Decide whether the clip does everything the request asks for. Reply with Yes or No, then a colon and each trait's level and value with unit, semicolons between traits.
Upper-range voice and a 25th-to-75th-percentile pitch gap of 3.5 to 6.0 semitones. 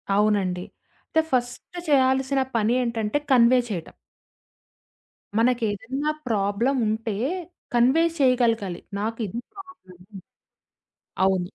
Yes: high, 230 Hz; average, 4.1 semitones